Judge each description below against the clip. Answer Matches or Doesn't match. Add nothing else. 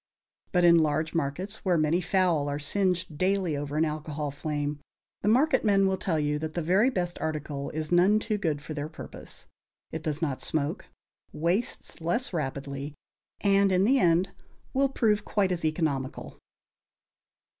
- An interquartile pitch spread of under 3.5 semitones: Doesn't match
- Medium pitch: Matches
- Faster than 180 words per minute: Doesn't match